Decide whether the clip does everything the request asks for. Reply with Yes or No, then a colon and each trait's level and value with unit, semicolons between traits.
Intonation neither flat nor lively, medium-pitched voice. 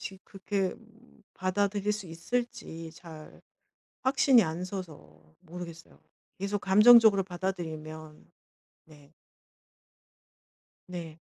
Yes: average, 3.9 semitones; medium, 180 Hz